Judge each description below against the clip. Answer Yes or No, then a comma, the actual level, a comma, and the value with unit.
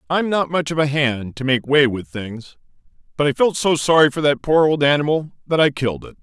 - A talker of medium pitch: Yes, medium, 145 Hz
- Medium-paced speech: No, fast, 240 wpm